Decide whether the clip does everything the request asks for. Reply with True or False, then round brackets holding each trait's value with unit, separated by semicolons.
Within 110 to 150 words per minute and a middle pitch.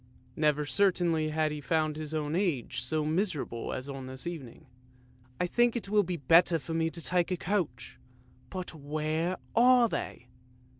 False (170 wpm; 160 Hz)